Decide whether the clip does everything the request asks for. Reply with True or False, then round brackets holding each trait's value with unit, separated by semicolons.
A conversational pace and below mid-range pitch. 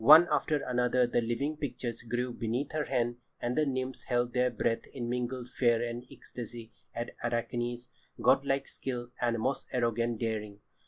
True (160 wpm; 120 Hz)